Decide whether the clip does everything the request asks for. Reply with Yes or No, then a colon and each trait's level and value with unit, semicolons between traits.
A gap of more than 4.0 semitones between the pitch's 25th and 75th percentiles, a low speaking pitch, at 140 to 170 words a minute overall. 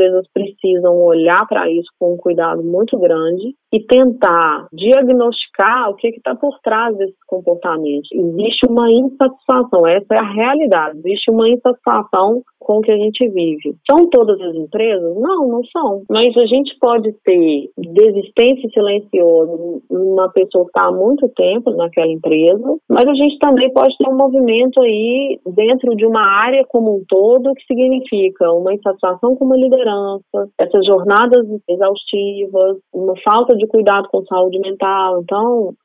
No: average, 5.1 semitones; high, 210 Hz; average, 150 wpm